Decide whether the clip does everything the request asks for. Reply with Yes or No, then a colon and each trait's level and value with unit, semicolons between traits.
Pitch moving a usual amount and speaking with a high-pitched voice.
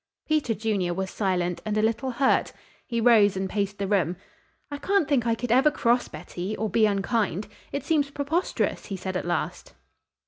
Yes: average, 5.0 semitones; high, 215 Hz